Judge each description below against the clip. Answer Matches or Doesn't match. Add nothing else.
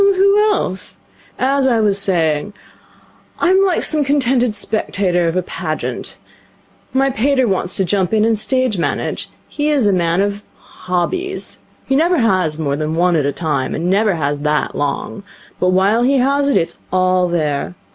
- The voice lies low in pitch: Doesn't match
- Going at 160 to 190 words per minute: Matches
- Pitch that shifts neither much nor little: Doesn't match